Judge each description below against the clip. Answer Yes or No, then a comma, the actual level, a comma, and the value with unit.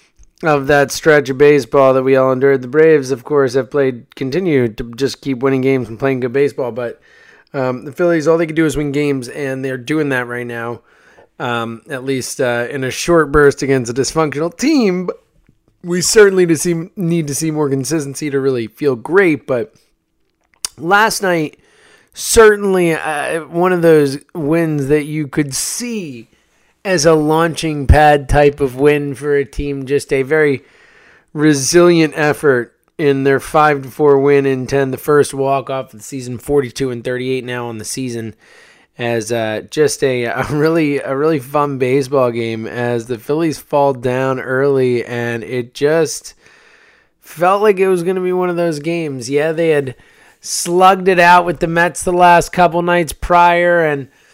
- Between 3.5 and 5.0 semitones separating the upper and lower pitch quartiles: Yes, average, 4.0 semitones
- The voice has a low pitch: No, medium, 145 Hz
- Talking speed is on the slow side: No, average, 185 wpm